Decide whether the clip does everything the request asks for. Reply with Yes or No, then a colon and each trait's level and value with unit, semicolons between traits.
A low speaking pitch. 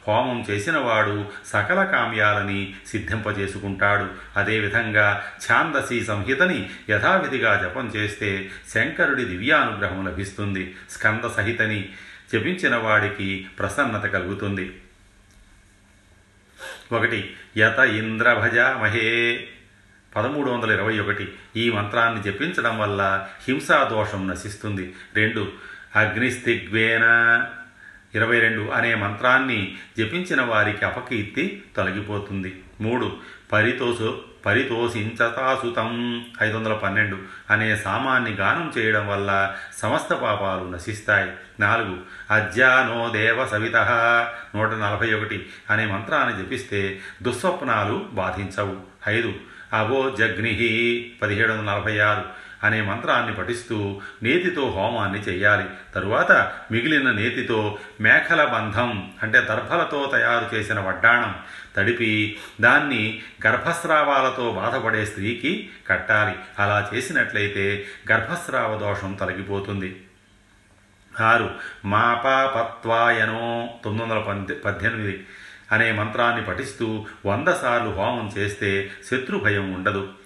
Yes: low, 105 Hz